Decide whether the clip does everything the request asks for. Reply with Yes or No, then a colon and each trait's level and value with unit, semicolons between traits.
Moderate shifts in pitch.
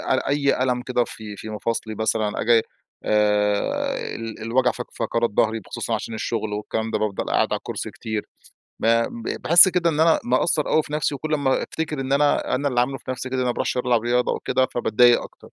Yes: average, 3.5 semitones